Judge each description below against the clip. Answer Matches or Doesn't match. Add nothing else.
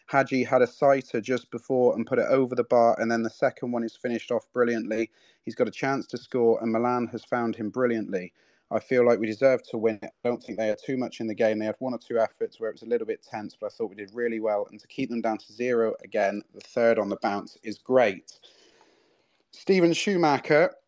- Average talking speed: Doesn't match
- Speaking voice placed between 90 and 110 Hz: Doesn't match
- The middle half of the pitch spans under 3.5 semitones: Matches